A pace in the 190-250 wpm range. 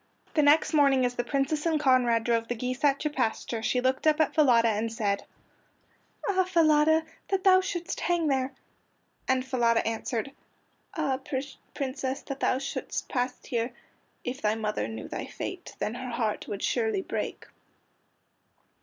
No: average, 160 wpm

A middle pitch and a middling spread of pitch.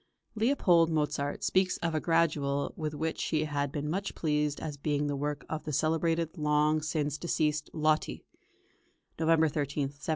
No: medium, 155 Hz; narrow, 1.8 semitones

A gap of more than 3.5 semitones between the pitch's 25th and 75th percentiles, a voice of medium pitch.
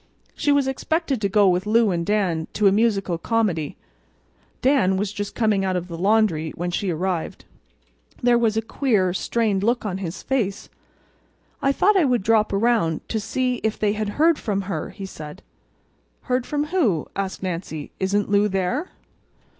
No: average, 4.1 semitones; high, 205 Hz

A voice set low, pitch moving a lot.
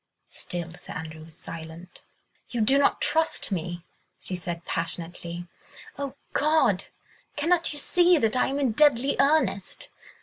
No: high, 215 Hz; wide, 9.0 semitones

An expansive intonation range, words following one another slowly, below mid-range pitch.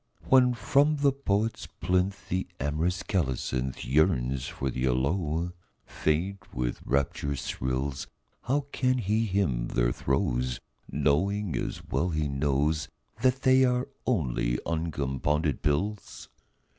Yes: wide, 7.1 semitones; slow, 120 wpm; very low, 80 Hz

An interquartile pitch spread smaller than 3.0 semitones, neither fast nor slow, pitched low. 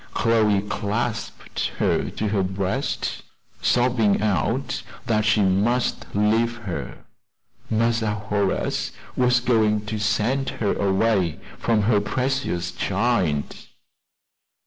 No: narrow, 2.6 semitones; slow, 100 wpm; low, 105 Hz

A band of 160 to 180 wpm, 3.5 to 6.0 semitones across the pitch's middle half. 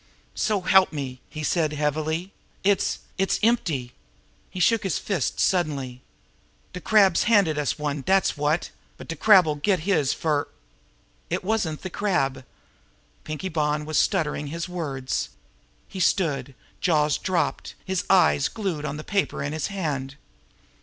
No: average, 150 wpm; average, 4.5 semitones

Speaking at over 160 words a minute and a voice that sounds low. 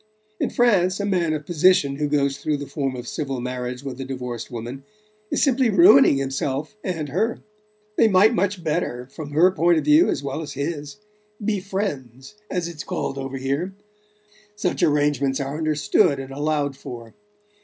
No: average, 175 wpm; medium, 145 Hz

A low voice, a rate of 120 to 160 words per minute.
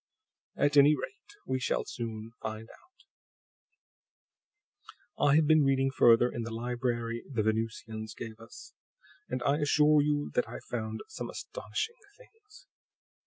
Yes: low, 125 Hz; slow, 135 wpm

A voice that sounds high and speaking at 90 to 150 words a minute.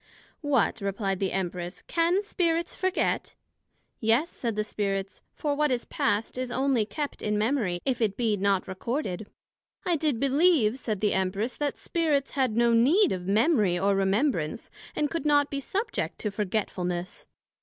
No: high, 230 Hz; average, 160 wpm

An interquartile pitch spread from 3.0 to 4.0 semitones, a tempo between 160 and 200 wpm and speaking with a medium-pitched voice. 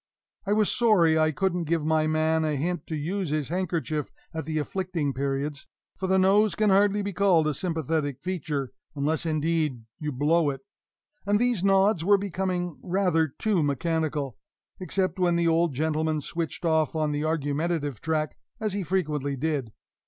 Yes: average, 3.7 semitones; average, 165 wpm; medium, 160 Hz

